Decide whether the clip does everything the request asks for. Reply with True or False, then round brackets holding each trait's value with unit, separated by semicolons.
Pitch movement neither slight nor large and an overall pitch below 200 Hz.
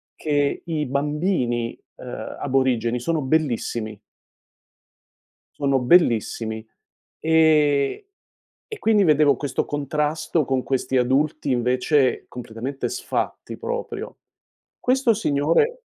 True (4.0 semitones; 140 Hz)